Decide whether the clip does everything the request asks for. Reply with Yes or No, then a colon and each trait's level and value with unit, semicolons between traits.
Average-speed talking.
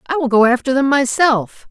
No: fast, 210 wpm